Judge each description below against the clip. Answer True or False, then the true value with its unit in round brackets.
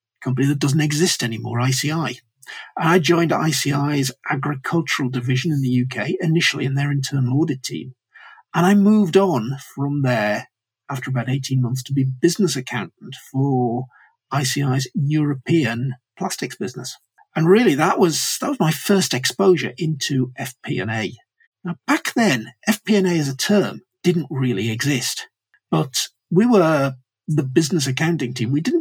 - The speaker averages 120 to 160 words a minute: True (150 wpm)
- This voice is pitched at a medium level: True (145 Hz)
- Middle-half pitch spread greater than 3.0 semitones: True (4.8 semitones)